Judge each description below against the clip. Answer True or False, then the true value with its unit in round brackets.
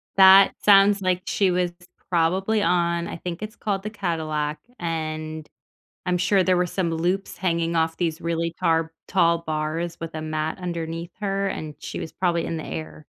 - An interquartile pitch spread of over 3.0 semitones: False (2.5 semitones)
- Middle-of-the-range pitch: True (170 Hz)